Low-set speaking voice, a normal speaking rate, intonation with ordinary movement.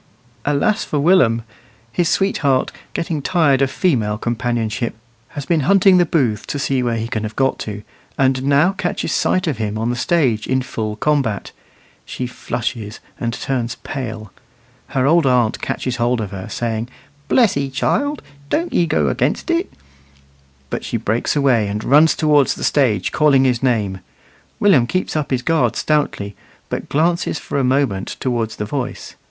Yes: low, 130 Hz; average, 170 wpm; average, 5.0 semitones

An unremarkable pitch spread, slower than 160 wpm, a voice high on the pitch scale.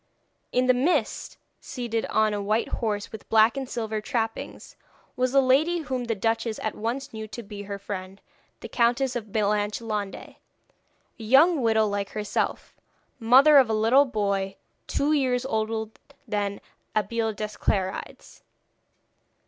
Yes: average, 3.1 semitones; average, 145 wpm; high, 225 Hz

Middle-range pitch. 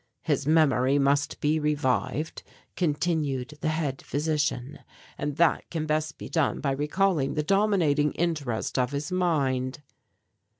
Yes: medium, 150 Hz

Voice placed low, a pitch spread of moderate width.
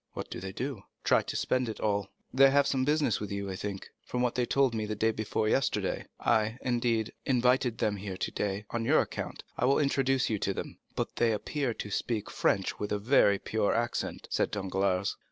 Yes: low, 110 Hz; average, 3.8 semitones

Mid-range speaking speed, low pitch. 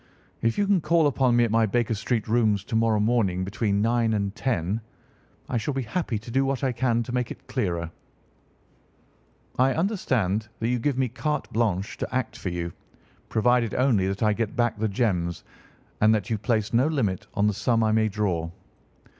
Yes: average, 195 wpm; low, 115 Hz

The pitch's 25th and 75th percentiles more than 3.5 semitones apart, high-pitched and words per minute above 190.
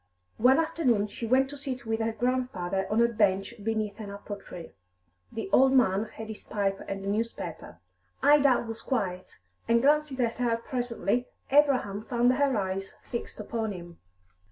No: average, 4.1 semitones; high, 225 Hz; average, 165 wpm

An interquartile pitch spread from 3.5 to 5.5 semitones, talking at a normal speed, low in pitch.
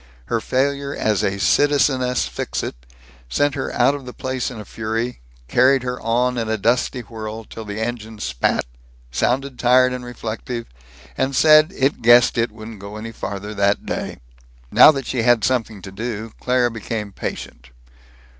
No: average, 2.8 semitones; average, 165 wpm; low, 120 Hz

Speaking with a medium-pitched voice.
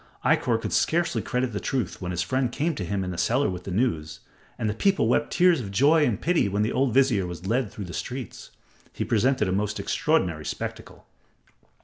No: low, 110 Hz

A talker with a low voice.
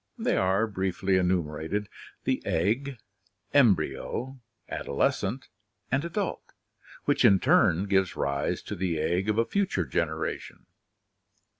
Yes: very low, 95 Hz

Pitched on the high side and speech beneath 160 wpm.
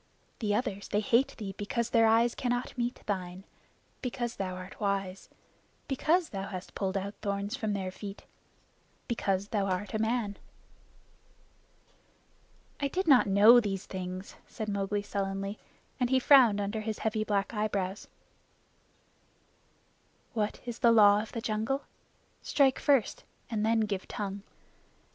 Yes: high, 210 Hz; average, 140 wpm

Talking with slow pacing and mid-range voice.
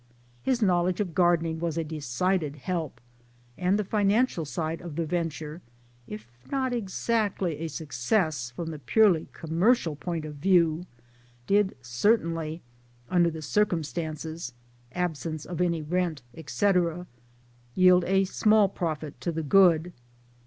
Yes: slow, 130 wpm; medium, 170 Hz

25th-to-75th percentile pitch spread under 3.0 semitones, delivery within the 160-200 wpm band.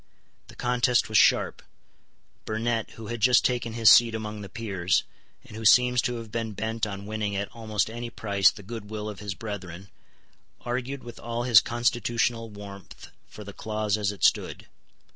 Yes: narrow, 2.5 semitones; average, 180 wpm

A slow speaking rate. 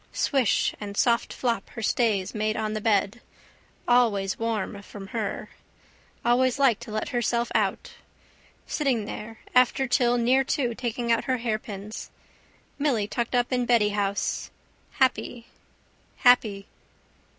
Yes: slow, 130 wpm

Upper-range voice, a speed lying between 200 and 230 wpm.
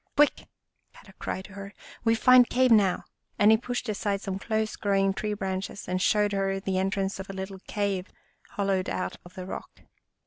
Yes: high, 200 Hz; fast, 205 wpm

